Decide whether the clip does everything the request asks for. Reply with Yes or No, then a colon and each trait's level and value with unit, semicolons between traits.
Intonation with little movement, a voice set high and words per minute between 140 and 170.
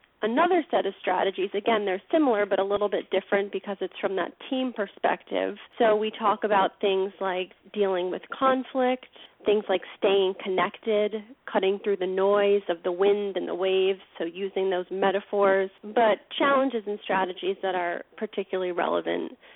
Yes: narrow, 2.2 semitones; high, 200 Hz; average, 165 wpm